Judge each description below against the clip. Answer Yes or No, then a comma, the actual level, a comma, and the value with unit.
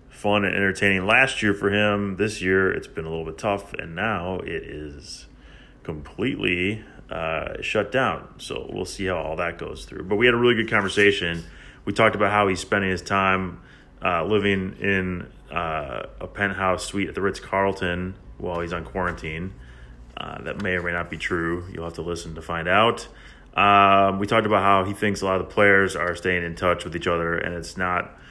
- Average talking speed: No, fast, 210 wpm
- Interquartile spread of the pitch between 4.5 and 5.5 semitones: No, average, 2.8 semitones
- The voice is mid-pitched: No, very low, 95 Hz